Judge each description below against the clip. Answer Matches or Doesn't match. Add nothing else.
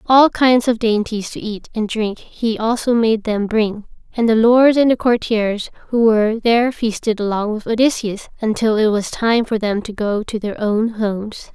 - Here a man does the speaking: Doesn't match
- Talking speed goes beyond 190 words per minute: Matches